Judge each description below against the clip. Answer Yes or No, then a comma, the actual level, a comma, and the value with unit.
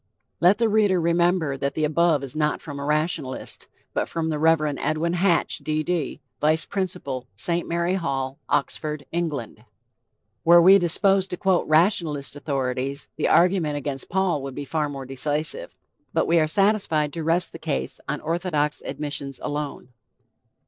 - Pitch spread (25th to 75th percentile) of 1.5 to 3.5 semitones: Yes, average, 3.2 semitones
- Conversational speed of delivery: Yes, average, 160 wpm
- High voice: No, medium, 155 Hz